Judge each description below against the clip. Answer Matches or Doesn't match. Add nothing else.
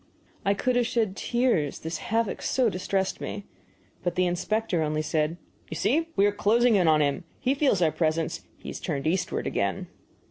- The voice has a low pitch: Doesn't match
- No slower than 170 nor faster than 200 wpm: Matches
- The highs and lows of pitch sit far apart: Matches